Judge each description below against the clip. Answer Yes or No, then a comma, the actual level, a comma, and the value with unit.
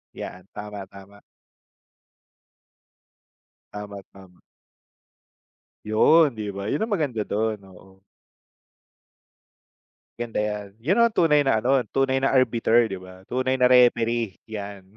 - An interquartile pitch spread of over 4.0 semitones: Yes, average, 4.5 semitones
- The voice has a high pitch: No, low, 110 Hz